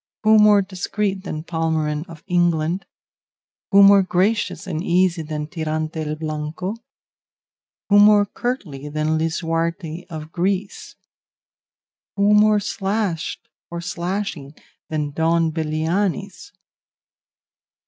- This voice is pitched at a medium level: Yes, medium, 170 Hz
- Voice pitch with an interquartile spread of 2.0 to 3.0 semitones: No, average, 4.0 semitones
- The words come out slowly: Yes, slow, 105 wpm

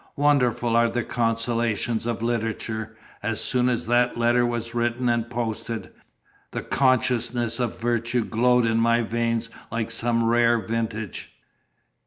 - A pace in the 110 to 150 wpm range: Yes, slow, 135 wpm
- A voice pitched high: No, low, 115 Hz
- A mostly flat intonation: Yes, narrow, 1.0 semitones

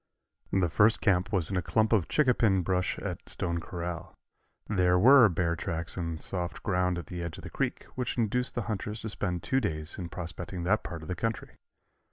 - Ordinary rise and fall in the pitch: Yes, average, 3.9 semitones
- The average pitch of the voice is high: No, very low, 90 Hz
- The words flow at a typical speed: No, fast, 210 wpm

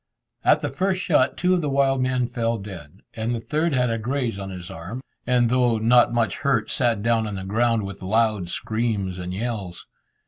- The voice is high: No, low, 115 Hz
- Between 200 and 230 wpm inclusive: Yes, fast, 205 wpm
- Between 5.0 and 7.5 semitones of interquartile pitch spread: No, average, 4.1 semitones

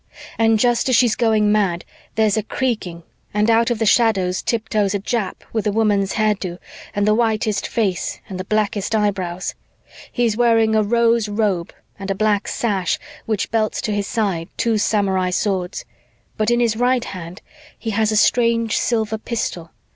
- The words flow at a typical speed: Yes, average, 170 wpm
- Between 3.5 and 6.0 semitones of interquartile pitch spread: No, narrow, 2.4 semitones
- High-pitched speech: Yes, high, 215 Hz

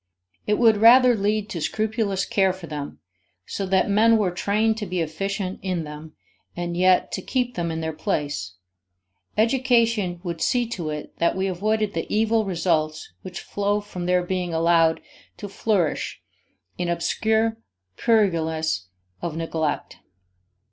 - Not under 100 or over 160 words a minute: Yes, average, 150 wpm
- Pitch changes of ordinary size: Yes, average, 4.5 semitones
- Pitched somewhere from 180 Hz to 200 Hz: Yes, medium, 185 Hz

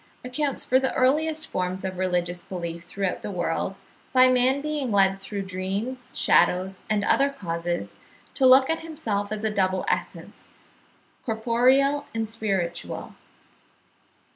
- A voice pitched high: Yes, high, 215 Hz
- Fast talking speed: No, average, 140 wpm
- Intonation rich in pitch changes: Yes, wide, 5.7 semitones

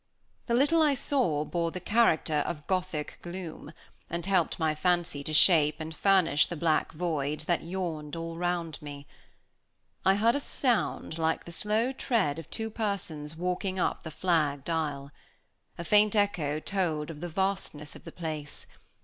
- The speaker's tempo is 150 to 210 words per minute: Yes, average, 165 wpm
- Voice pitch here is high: No, medium, 170 Hz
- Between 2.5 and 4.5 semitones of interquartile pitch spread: Yes, average, 4.0 semitones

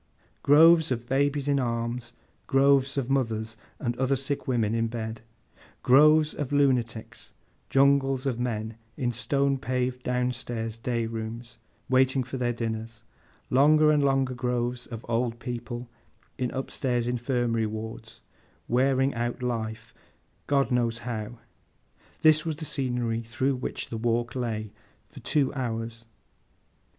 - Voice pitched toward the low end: Yes, low, 125 Hz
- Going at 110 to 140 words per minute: Yes, slow, 135 wpm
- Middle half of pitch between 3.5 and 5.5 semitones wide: No, average, 2.7 semitones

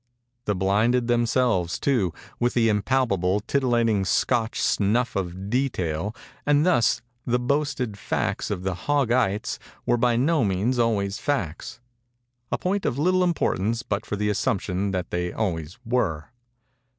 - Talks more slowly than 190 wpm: Yes, average, 140 wpm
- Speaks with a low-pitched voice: Yes, low, 115 Hz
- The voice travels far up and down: No, average, 4.2 semitones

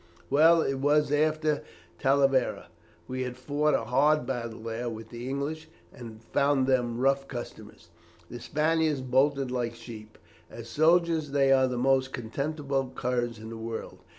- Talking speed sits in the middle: Yes, average, 150 wpm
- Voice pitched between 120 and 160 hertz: Yes, low, 135 Hz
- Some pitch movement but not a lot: Yes, average, 3.4 semitones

